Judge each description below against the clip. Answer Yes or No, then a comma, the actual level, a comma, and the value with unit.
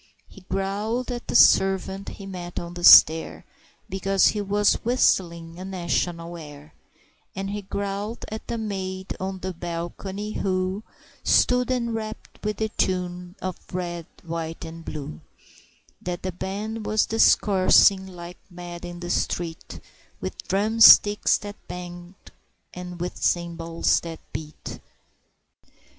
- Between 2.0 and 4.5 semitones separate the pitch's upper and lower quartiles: Yes, average, 2.8 semitones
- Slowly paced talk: Yes, slow, 130 wpm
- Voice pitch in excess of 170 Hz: Yes, medium, 185 Hz